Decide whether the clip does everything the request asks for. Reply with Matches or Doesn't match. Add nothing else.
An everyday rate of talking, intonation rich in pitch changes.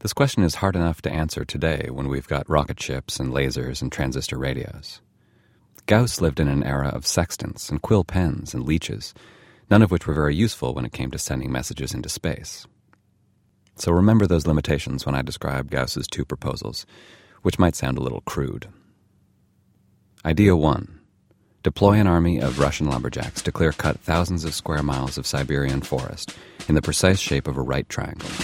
Matches